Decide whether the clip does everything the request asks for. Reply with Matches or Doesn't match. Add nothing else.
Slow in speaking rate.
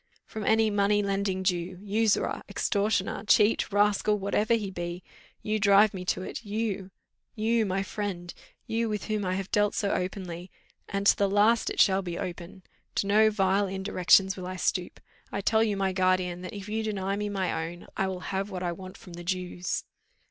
Doesn't match